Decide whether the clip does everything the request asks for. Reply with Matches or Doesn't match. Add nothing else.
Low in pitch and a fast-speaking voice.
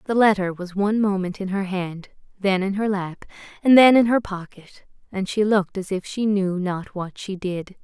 Doesn't match